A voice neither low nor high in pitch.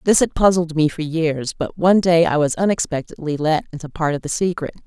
Yes: medium, 160 Hz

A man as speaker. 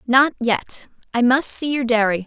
No: female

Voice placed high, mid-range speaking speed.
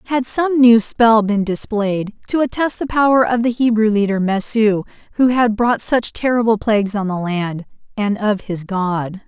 Yes: high, 220 Hz; average, 175 wpm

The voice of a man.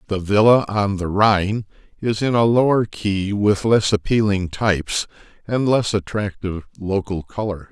Yes: male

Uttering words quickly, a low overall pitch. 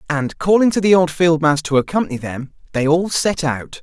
No: fast, 220 wpm; medium, 160 Hz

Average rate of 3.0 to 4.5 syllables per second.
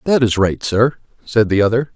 No: 5.2 syllables/s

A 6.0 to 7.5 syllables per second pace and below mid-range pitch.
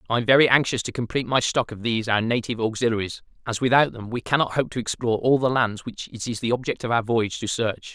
Yes: 6.7 syllables/s; low, 120 Hz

